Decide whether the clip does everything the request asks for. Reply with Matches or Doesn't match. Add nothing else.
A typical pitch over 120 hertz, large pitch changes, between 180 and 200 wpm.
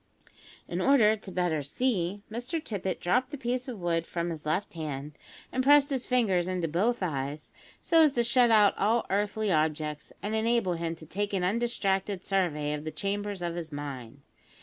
Matches